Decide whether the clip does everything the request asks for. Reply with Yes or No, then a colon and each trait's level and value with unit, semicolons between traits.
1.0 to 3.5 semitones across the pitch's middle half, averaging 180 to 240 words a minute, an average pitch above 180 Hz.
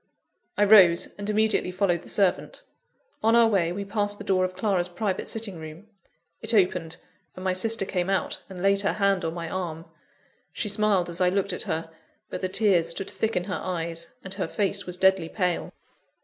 Yes: narrow, 2.6 semitones; average, 200 wpm; high, 190 Hz